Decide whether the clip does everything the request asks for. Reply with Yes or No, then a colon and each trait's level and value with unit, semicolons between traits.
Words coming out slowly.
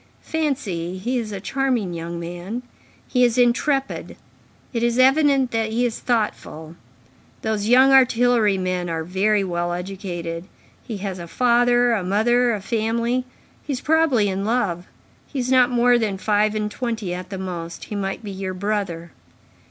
No: average, 165 wpm